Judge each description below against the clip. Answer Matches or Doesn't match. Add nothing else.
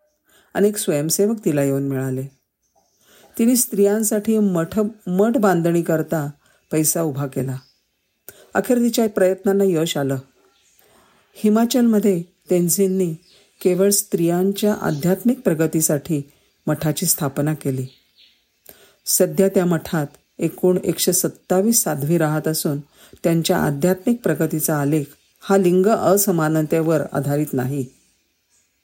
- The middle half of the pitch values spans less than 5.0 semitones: Doesn't match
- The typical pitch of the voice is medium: Matches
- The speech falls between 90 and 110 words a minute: Matches